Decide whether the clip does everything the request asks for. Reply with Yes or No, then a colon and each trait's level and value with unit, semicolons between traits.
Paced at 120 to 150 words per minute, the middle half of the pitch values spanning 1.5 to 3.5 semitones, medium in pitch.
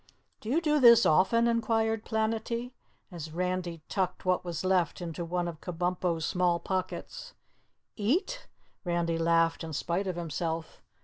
No: average, 140 wpm; average, 4.9 semitones; medium, 180 Hz